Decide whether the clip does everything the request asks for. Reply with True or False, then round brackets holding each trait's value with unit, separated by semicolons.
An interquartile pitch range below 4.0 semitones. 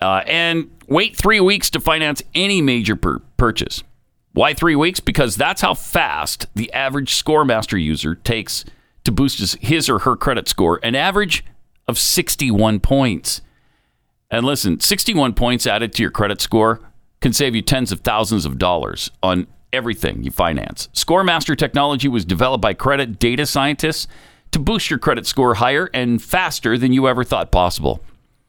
False (5.2 semitones)